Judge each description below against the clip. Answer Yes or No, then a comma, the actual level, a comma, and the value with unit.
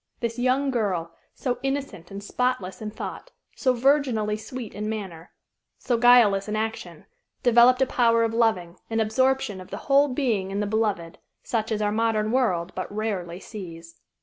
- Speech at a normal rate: Yes, average, 170 wpm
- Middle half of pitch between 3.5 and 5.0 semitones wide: Yes, average, 4.0 semitones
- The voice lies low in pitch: No, high, 220 Hz